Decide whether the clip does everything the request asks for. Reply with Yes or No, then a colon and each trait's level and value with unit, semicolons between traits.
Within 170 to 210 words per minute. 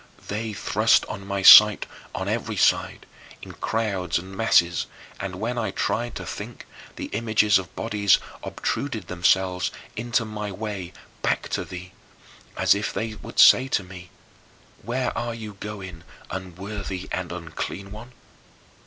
No: average, 145 wpm